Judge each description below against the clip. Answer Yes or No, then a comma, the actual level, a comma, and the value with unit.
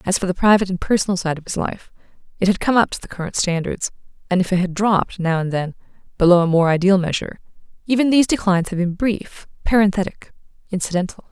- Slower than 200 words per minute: No, fast, 205 wpm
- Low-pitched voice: No, high, 190 Hz